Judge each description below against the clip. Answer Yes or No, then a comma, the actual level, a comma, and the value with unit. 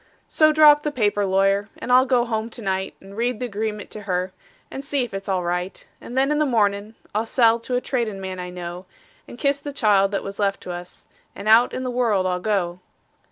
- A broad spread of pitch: No, average, 4.4 semitones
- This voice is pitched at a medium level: No, high, 210 Hz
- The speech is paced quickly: Yes, fast, 240 wpm